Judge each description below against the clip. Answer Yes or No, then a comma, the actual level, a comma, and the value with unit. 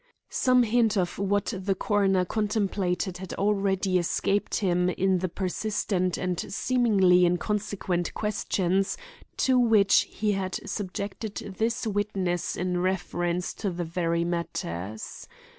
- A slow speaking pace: Yes, slow, 120 wpm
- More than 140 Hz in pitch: Yes, high, 190 Hz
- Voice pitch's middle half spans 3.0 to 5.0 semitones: No, narrow, 2.6 semitones